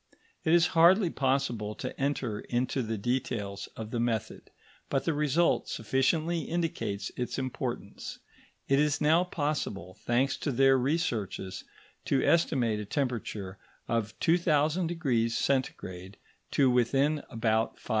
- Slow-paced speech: Yes, slow, 125 wpm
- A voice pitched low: Yes, low, 130 Hz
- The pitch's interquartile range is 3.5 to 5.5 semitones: Yes, average, 5.2 semitones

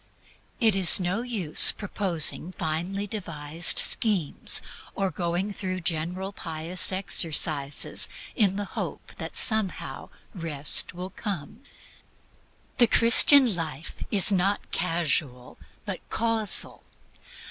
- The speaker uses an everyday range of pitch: Yes, average, 4.0 semitones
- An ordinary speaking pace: No, slow, 105 wpm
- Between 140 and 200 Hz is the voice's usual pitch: Yes, medium, 185 Hz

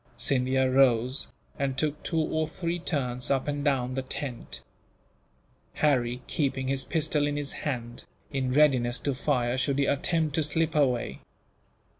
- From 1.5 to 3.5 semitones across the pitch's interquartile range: Yes, narrow, 2.6 semitones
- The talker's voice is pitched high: No, low, 135 Hz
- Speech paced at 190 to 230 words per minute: No, average, 150 wpm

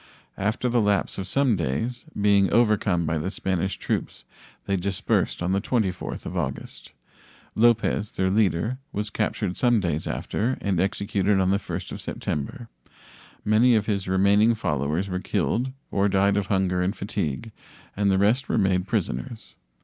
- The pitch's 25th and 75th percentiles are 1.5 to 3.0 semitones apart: Yes, average, 2.7 semitones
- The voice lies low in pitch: Yes, low, 100 Hz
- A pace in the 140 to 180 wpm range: Yes, average, 160 wpm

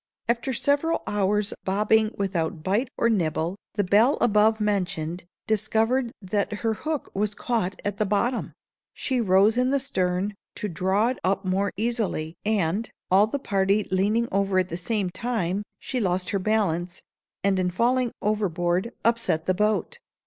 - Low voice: No, high, 205 Hz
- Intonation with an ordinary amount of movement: Yes, average, 3.4 semitones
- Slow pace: No, average, 155 wpm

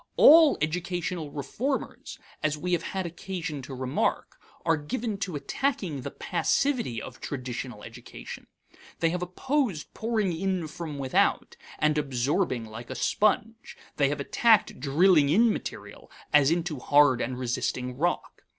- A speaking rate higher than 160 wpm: No, average, 140 wpm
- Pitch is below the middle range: No, medium, 160 Hz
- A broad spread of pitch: Yes, wide, 5.7 semitones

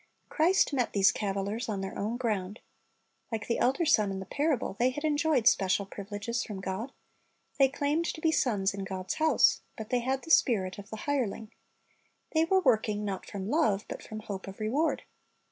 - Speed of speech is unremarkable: Yes, average, 190 wpm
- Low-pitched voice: No, high, 220 Hz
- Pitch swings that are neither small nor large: No, wide, 6.0 semitones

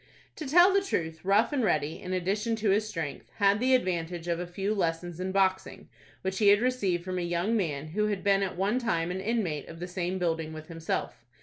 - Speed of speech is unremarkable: No, fast, 225 wpm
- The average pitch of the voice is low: No, medium, 185 Hz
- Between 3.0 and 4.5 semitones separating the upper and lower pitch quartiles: Yes, average, 3.8 semitones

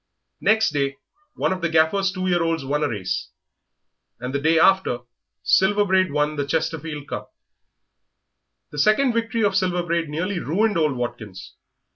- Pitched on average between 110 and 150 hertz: No, medium, 165 Hz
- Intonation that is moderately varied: Yes, average, 4.7 semitones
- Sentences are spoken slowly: No, average, 160 wpm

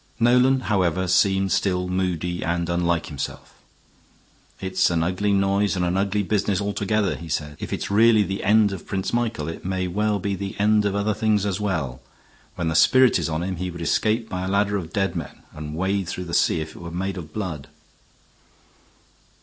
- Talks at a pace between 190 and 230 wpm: Yes, average, 200 wpm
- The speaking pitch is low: Yes, very low, 95 Hz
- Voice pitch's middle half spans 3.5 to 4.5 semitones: No, average, 2.9 semitones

